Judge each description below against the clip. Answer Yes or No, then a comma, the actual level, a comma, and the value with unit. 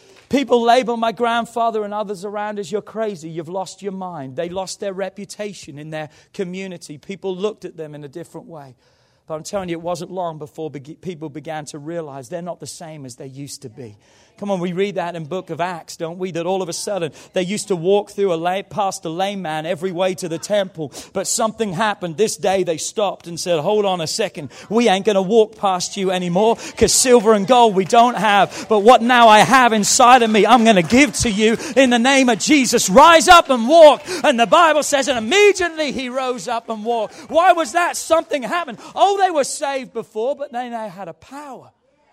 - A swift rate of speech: Yes, fast, 225 wpm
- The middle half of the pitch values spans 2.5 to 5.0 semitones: No, wide, 5.6 semitones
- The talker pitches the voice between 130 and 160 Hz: No, high, 200 Hz